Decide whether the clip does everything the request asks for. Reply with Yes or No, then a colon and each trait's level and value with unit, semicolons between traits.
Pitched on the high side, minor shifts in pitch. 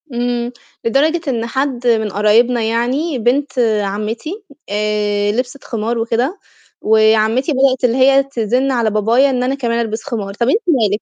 No: high, 240 Hz; average, 3.3 semitones